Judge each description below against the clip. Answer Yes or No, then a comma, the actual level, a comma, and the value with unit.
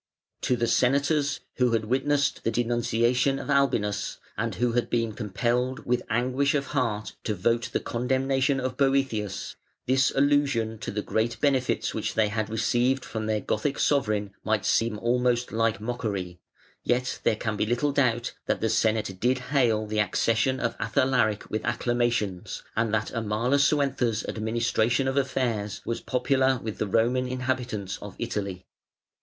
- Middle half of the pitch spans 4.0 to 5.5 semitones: No, average, 3.2 semitones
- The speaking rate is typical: Yes, average, 155 wpm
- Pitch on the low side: Yes, low, 120 Hz